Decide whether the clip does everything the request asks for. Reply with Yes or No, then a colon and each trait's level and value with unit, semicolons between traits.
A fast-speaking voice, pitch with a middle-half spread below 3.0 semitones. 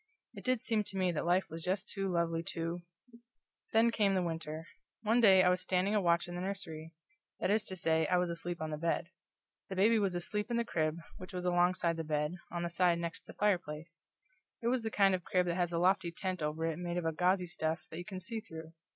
Yes: fast, 240 wpm; narrow, 2.6 semitones